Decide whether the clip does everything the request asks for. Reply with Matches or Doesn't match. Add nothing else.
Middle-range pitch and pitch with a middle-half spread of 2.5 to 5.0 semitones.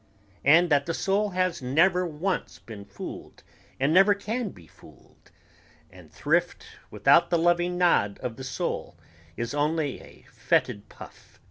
Doesn't match